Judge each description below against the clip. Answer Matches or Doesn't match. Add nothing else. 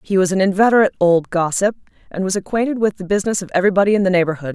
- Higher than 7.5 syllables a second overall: Matches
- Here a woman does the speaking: Matches